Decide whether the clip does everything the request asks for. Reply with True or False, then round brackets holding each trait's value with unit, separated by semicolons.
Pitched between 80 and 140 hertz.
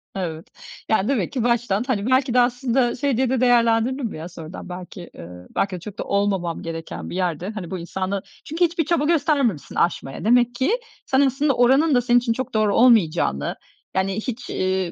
False (225 Hz)